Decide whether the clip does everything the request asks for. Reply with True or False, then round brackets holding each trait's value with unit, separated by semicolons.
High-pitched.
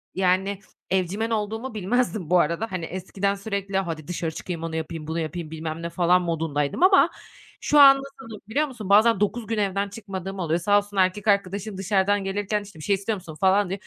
True (195 Hz)